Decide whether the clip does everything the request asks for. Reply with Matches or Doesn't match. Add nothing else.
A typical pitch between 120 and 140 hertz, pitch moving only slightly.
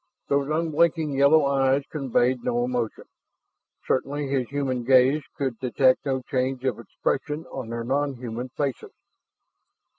Matches